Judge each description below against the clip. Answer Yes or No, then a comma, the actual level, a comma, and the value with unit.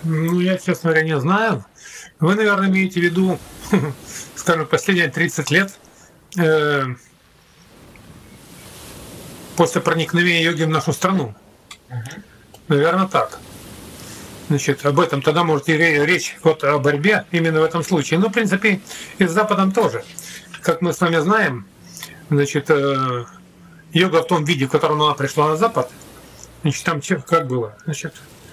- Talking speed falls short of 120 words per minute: No, average, 140 wpm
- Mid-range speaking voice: Yes, medium, 165 Hz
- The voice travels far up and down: No, average, 3.3 semitones